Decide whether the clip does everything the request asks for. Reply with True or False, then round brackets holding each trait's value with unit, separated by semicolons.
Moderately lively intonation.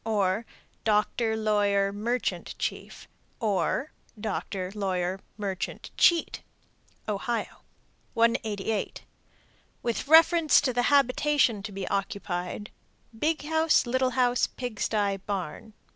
True (3.9 semitones)